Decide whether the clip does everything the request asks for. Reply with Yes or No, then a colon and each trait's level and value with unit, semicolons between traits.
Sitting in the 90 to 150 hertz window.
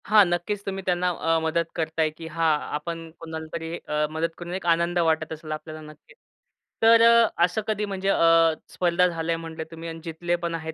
No: medium, 165 Hz